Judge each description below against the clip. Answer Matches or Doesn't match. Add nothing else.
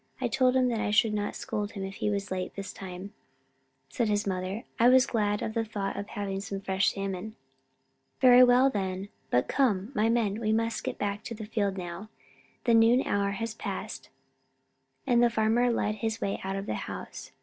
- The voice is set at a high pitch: Matches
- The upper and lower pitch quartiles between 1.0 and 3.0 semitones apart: Matches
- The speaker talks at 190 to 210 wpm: Matches